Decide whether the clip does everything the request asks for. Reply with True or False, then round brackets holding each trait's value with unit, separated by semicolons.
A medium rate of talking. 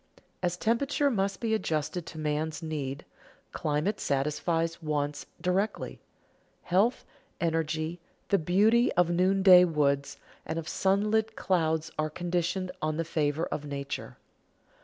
False (120 wpm)